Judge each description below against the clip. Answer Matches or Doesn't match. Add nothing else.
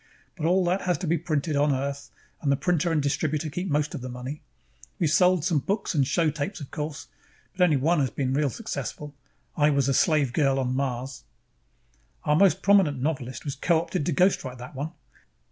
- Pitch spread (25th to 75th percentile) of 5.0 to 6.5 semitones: Doesn't match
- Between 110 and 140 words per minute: Doesn't match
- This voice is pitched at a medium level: Matches